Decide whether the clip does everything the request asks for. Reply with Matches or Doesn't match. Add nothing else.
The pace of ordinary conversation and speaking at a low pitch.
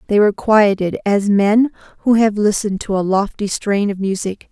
Doesn't match